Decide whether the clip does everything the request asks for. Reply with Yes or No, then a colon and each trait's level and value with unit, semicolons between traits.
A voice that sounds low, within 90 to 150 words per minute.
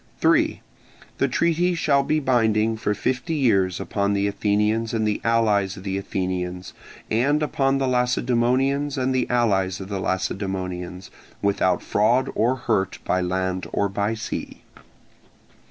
Yes: low, 110 Hz; average, 140 wpm